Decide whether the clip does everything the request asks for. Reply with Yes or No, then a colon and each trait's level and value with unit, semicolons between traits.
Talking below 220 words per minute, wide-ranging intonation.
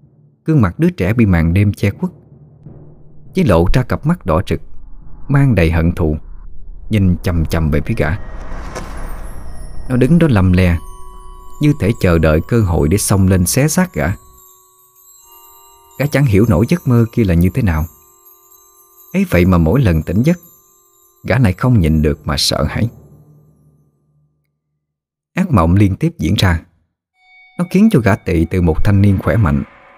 Yes: average, 170 wpm; wide, 8.3 semitones